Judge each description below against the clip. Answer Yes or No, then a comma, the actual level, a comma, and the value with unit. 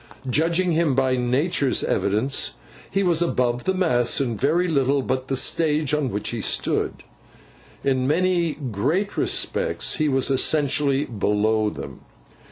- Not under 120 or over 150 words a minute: Yes, average, 140 wpm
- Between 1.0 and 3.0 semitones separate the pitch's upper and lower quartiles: No, average, 4.6 semitones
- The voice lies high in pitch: No, medium, 140 Hz